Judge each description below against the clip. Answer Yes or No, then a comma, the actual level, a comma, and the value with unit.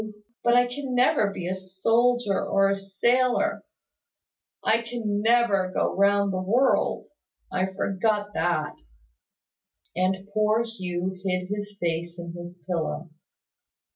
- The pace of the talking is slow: Yes, slow, 125 wpm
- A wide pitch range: No, average, 3.6 semitones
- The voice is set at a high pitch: Yes, high, 195 Hz